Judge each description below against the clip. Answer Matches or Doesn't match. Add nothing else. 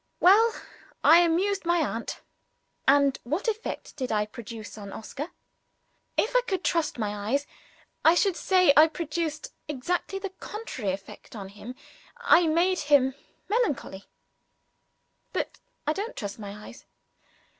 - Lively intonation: Matches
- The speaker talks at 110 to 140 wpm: Matches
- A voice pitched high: Matches